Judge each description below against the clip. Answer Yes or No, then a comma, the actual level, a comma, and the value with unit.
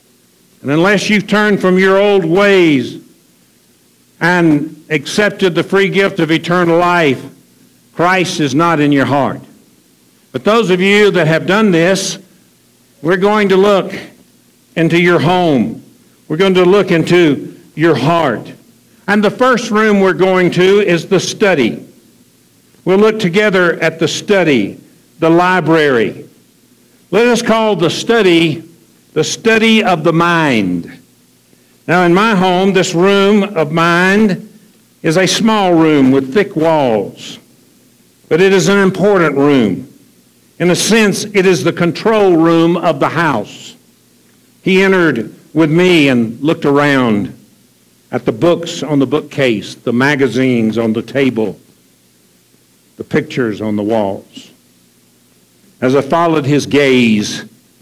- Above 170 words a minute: No, slow, 135 wpm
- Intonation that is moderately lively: Yes, average, 5.0 semitones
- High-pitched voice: No, medium, 170 Hz